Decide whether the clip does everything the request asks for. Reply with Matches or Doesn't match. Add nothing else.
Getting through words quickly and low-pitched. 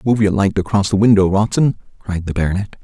Matches